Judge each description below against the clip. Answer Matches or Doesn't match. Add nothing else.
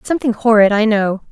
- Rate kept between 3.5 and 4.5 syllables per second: Doesn't match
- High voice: Matches